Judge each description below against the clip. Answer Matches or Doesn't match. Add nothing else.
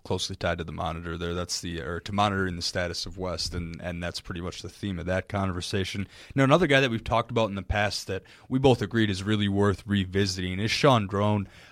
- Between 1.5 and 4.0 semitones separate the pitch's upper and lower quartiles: Matches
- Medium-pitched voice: Doesn't match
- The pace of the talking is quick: Matches